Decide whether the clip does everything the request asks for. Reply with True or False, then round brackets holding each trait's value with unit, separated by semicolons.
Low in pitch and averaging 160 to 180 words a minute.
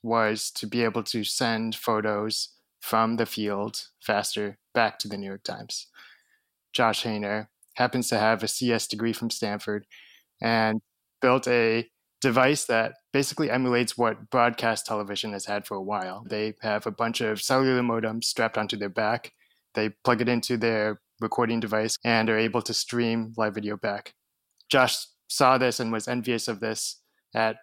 True (115 Hz; 165 wpm)